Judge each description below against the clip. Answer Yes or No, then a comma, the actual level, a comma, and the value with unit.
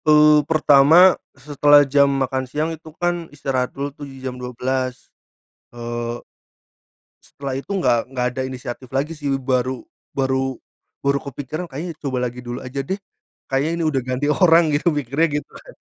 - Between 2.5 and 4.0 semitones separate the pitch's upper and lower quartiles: Yes, average, 2.8 semitones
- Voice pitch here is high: No, low, 135 Hz